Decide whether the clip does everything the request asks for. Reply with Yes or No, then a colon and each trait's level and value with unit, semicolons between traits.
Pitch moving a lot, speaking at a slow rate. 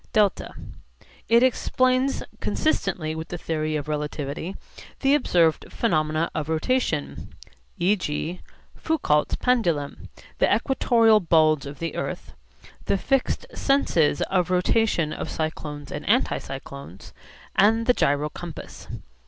Yes: wide, 7.0 semitones; slow, 110 wpm